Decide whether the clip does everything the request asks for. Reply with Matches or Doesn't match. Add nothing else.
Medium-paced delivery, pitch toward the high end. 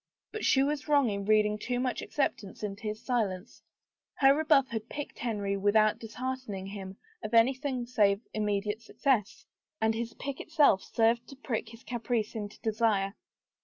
Matches